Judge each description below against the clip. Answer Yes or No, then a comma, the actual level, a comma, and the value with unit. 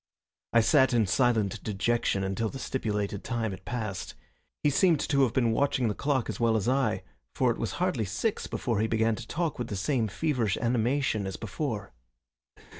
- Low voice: Yes, low, 115 Hz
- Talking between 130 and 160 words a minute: No, average, 190 wpm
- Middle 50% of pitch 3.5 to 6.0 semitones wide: Yes, average, 3.8 semitones